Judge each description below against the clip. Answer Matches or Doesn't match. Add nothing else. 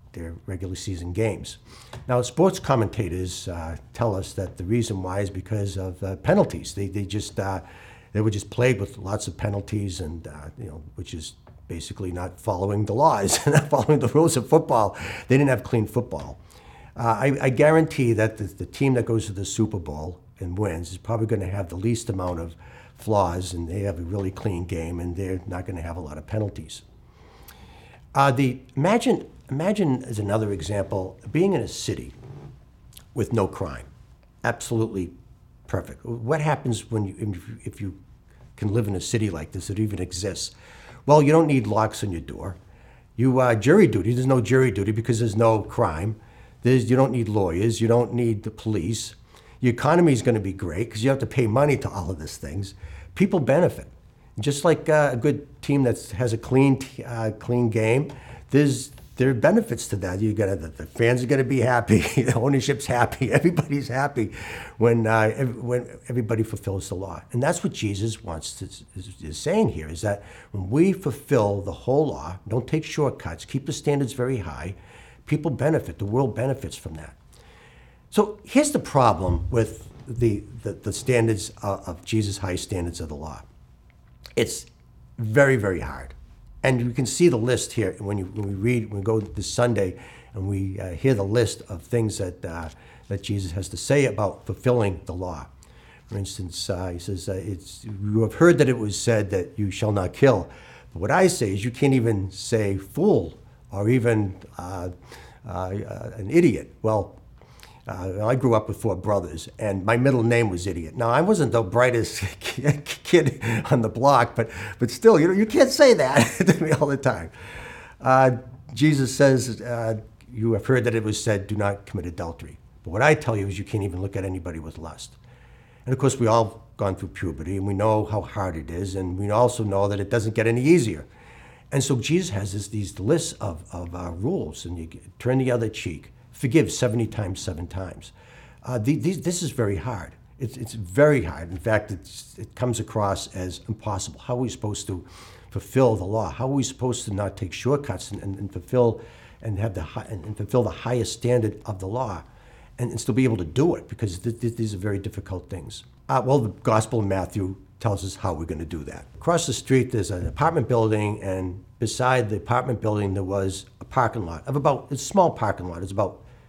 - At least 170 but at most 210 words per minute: Matches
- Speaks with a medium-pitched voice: Doesn't match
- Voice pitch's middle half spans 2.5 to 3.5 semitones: Doesn't match